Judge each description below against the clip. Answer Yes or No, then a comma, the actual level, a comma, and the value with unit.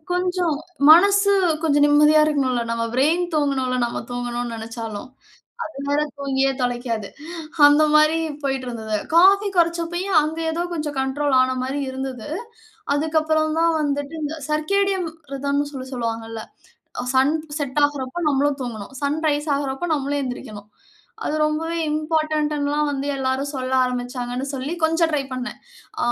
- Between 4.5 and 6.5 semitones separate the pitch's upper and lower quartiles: No, average, 3.4 semitones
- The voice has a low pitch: No, very high, 285 Hz